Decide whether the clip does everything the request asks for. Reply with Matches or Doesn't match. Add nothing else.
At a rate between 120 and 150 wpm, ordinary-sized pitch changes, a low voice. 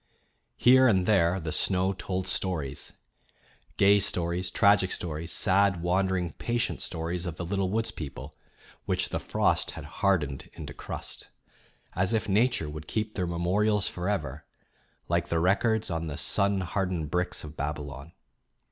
Matches